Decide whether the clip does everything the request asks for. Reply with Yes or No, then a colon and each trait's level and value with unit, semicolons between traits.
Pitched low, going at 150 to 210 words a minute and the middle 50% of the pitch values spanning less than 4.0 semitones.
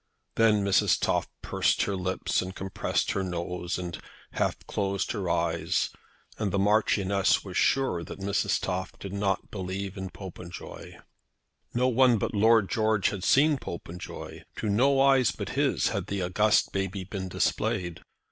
Yes: low, 100 Hz; average, 155 wpm; average, 2.8 semitones